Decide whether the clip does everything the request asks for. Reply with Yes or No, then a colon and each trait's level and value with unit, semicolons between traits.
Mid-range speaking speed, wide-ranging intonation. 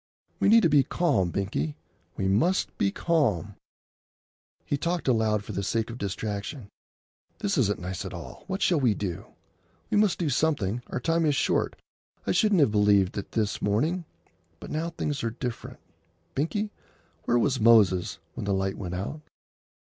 Yes: average, 170 wpm; wide, 8.0 semitones